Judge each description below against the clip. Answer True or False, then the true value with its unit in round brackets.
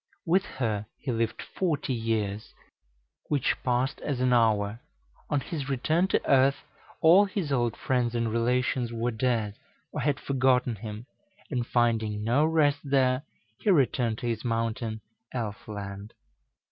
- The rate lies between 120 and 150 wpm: True (145 wpm)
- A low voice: True (120 Hz)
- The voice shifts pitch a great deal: False (3.5 semitones)